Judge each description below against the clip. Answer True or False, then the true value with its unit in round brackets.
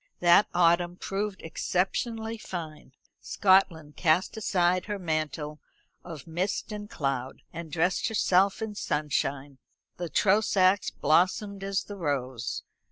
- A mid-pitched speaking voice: True (175 Hz)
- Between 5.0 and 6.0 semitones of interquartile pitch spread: False (4.3 semitones)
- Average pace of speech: False (115 wpm)